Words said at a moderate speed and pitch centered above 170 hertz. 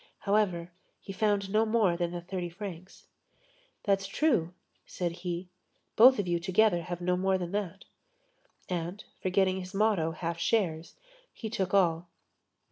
Yes: average, 145 wpm; medium, 185 Hz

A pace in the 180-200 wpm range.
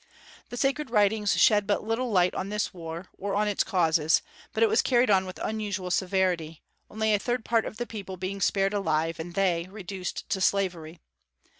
Yes: average, 190 wpm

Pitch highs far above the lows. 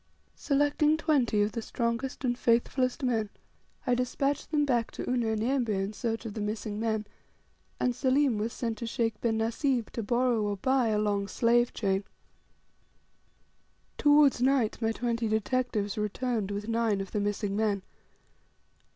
No: average, 3.1 semitones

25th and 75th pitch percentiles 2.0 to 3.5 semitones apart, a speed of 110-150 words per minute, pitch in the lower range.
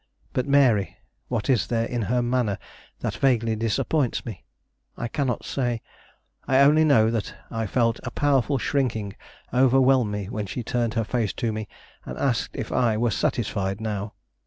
No: average, 2.8 semitones; average, 165 wpm; low, 115 Hz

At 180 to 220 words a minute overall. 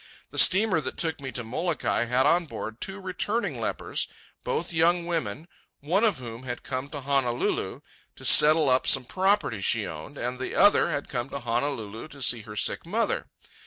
Yes: average, 185 wpm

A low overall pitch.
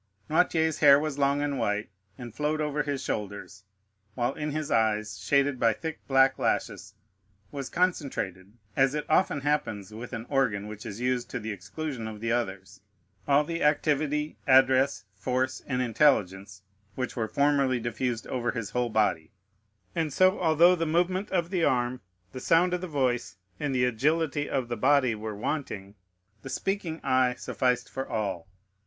Yes: low, 130 Hz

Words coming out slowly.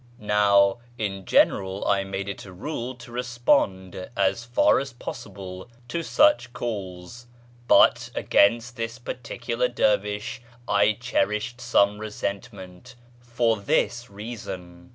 Yes: slow, 115 wpm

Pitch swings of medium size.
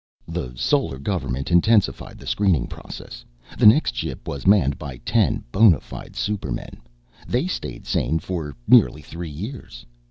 No: wide, 6.9 semitones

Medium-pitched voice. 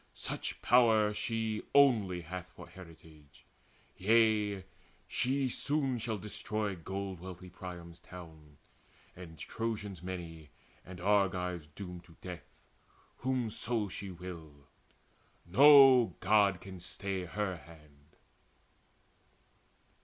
No: very low, 95 Hz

